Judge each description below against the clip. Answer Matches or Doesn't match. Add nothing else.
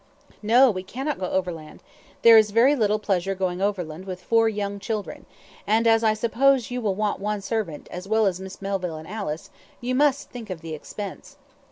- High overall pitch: Matches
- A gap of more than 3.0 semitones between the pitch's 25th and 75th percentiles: Matches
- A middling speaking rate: Matches